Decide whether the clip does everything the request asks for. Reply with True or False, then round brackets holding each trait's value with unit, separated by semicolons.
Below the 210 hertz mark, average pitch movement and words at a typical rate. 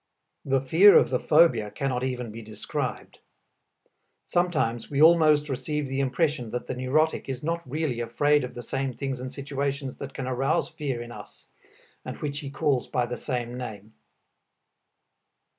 True (135 Hz; 3.2 semitones; 160 wpm)